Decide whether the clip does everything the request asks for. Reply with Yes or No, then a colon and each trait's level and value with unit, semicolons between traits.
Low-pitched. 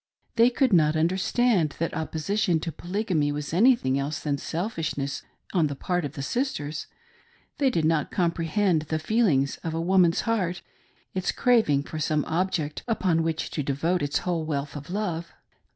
No: medium, 165 Hz